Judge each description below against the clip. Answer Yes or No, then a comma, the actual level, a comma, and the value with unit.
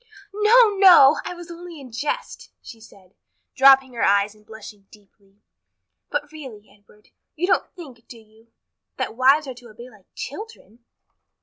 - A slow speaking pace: No, average, 160 wpm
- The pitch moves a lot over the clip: Yes, wide, 6.5 semitones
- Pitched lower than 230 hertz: No, very high, 250 Hz